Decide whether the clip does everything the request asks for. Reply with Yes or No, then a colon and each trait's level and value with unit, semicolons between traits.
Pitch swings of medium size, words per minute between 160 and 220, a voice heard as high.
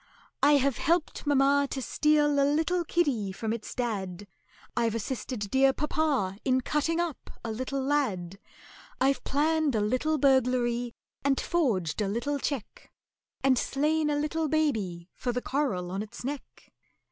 No: average, 4.7 semitones; average, 150 wpm; very high, 270 Hz